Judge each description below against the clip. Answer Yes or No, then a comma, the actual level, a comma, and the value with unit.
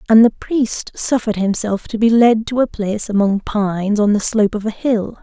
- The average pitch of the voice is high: Yes, high, 215 Hz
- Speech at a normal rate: No, fast, 220 wpm